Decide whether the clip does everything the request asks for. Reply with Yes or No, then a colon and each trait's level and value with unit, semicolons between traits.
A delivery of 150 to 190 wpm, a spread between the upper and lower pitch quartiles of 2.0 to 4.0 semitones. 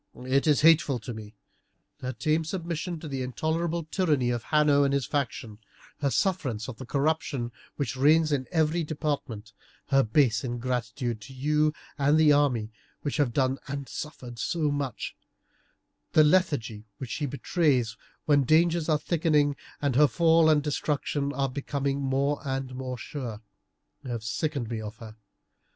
Yes: average, 155 wpm; average, 3.6 semitones